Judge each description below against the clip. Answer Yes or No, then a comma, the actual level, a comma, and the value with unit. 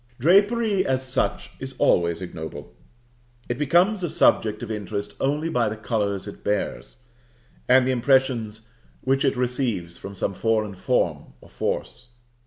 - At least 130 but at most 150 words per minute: Yes, average, 145 wpm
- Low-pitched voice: Yes, low, 120 Hz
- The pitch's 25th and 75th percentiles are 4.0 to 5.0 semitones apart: Yes, average, 4.6 semitones